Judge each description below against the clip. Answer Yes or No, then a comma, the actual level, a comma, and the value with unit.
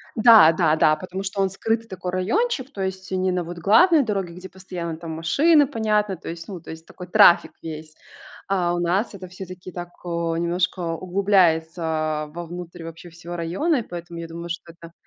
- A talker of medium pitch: Yes, medium, 180 Hz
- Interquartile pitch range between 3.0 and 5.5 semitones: No, narrow, 2.6 semitones